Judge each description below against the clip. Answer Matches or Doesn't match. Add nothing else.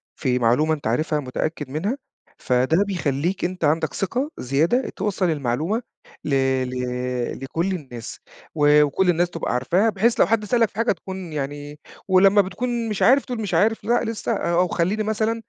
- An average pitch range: Doesn't match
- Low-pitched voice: Doesn't match